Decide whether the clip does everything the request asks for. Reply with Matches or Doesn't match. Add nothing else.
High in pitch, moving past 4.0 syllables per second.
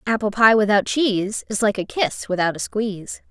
Matches